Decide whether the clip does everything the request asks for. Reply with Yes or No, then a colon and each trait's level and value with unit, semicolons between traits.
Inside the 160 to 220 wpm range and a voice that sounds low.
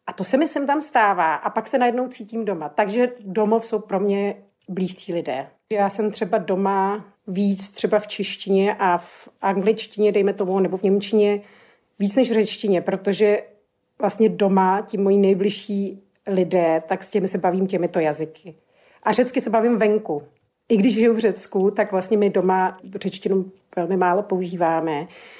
No: fast, 170 wpm; high, 200 Hz